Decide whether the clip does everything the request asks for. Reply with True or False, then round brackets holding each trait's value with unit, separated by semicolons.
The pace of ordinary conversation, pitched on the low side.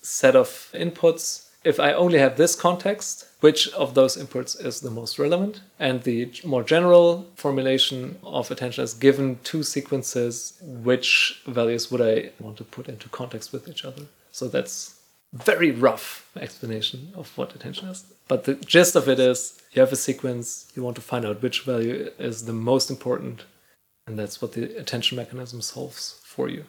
True (180 wpm; 130 Hz)